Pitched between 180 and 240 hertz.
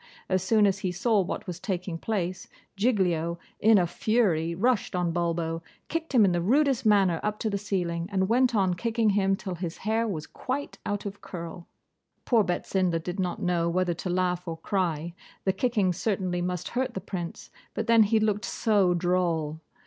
Yes: medium, 185 Hz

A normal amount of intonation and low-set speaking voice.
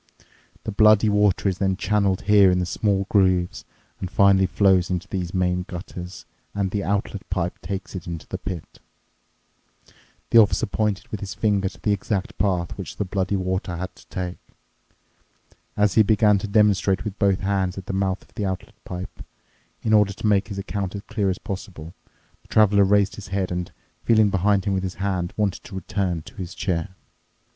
No: narrow, 1.8 semitones; very low, 95 Hz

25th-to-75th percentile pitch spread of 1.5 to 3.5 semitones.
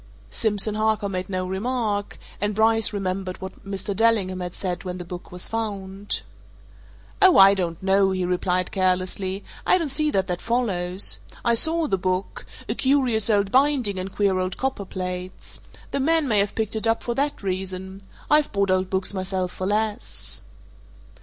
Yes: average, 3.2 semitones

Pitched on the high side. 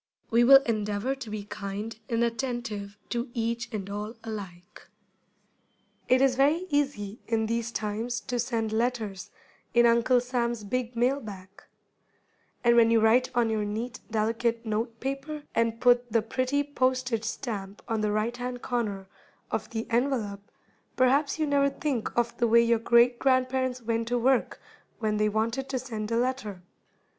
Yes: high, 235 Hz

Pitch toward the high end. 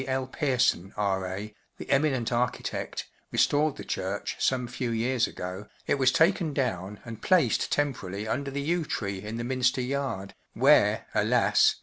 No: low, 125 Hz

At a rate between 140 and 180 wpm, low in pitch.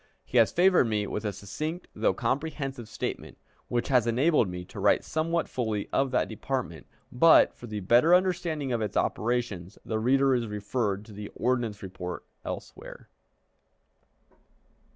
Yes: average, 150 wpm; low, 120 Hz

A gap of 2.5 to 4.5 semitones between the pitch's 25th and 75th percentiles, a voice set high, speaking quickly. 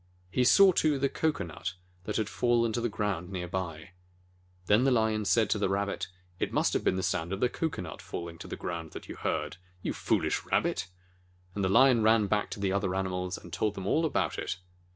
No: average, 4.1 semitones; low, 100 Hz; fast, 220 wpm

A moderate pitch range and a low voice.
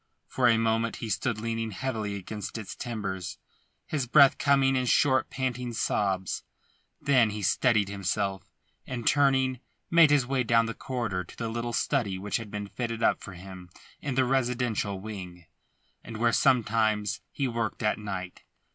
Yes: average, 3.9 semitones; low, 115 Hz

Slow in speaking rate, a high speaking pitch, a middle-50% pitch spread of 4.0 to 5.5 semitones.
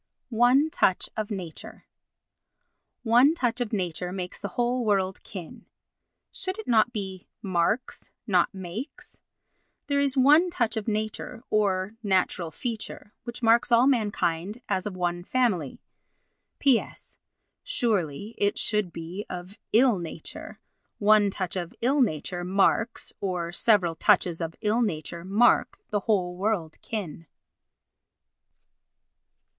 Yes: slow, 120 wpm; high, 205 Hz; average, 4.8 semitones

